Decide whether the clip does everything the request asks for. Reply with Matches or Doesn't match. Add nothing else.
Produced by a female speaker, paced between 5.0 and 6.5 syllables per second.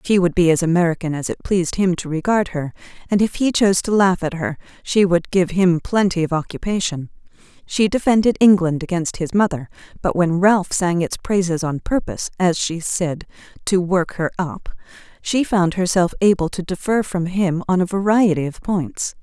Matches